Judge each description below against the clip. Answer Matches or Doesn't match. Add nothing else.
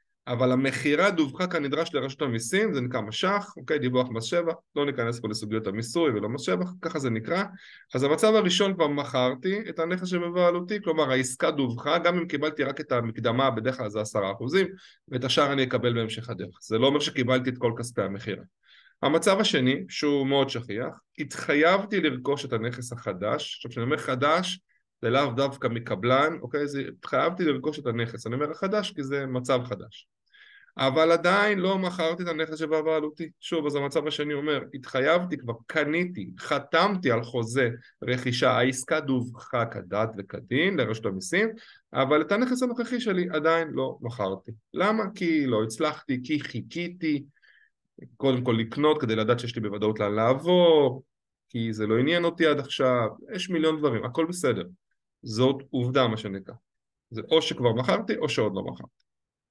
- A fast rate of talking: Matches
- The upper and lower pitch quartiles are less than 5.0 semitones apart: Doesn't match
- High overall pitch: Doesn't match